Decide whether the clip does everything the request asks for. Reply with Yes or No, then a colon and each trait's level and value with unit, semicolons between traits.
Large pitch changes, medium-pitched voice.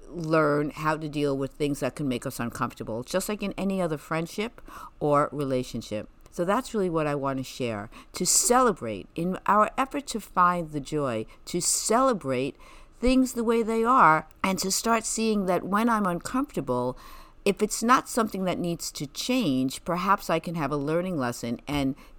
Yes: wide, 6.9 semitones; medium, 170 Hz